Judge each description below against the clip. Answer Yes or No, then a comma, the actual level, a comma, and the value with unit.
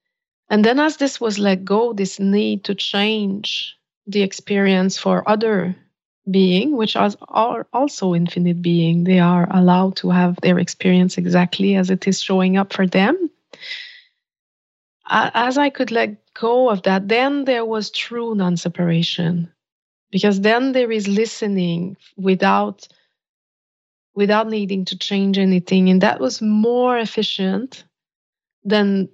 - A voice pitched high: Yes, high, 195 Hz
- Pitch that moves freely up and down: No, average, 3.3 semitones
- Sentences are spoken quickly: No, slow, 135 wpm